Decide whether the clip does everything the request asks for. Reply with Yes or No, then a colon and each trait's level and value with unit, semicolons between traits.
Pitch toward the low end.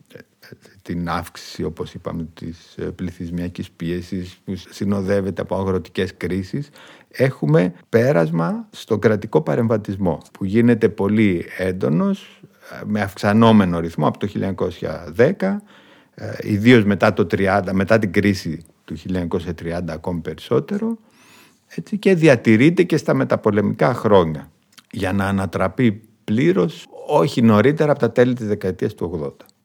Yes: low, 100 Hz